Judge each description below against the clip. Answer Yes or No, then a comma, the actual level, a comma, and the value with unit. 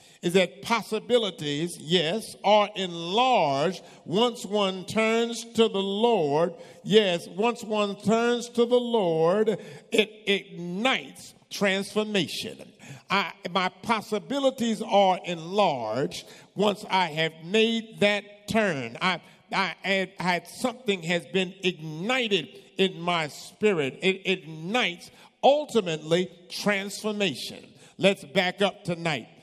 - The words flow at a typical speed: No, slow, 110 wpm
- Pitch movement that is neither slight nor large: Yes, average, 3.7 semitones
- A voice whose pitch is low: No, high, 200 Hz